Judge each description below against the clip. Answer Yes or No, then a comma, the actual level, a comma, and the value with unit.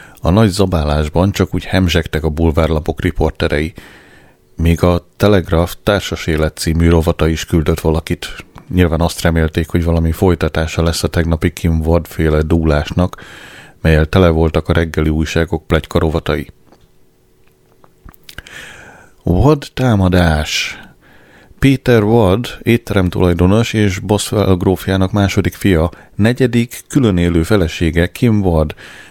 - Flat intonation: No, average, 3.2 semitones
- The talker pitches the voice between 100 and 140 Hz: No, very low, 85 Hz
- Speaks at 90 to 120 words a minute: Yes, average, 115 wpm